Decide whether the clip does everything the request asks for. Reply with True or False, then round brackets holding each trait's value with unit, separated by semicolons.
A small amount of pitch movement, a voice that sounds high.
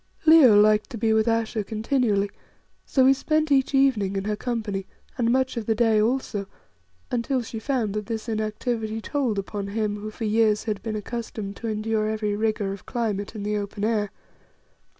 True (2.2 semitones; 220 Hz)